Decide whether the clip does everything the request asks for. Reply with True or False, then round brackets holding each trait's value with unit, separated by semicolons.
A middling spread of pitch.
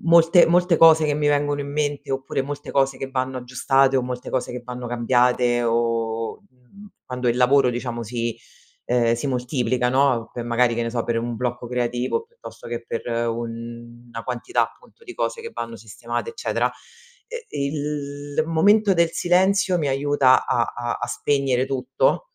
True (3.4 semitones)